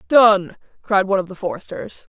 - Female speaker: Yes, female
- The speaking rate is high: No, average, 165 wpm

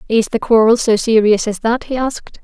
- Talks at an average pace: No, fast, 220 wpm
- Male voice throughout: No, female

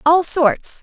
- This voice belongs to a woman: Yes, female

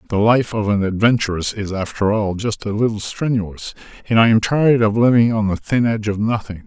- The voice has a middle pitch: No, low, 110 Hz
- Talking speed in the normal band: No, fast, 215 wpm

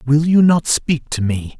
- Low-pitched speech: No, medium, 145 Hz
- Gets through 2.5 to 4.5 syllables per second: Yes, 4.1 syllables/s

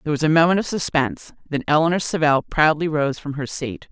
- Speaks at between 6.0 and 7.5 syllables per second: Yes, 6.1 syllables/s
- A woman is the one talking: Yes, female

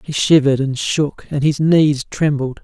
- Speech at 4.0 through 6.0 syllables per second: Yes, 4.4 syllables/s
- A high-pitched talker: No, medium, 145 Hz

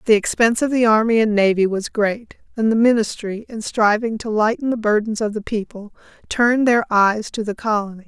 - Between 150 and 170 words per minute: No, average, 200 wpm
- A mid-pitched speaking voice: No, high, 220 Hz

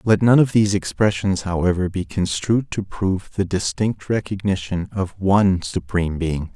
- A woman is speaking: No, male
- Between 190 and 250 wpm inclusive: No, average, 155 wpm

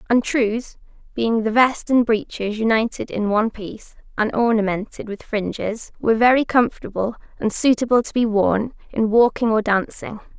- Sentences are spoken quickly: No, average, 155 wpm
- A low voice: No, high, 225 Hz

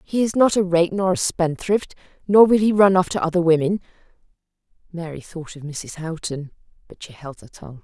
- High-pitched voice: No, medium, 175 Hz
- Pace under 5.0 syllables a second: No, 5.4 syllables/s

